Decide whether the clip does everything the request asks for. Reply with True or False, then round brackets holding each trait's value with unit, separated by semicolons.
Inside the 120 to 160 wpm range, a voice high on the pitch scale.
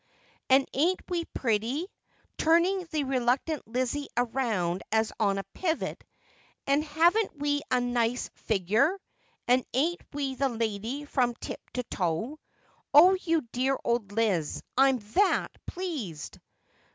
True (135 wpm; 265 Hz)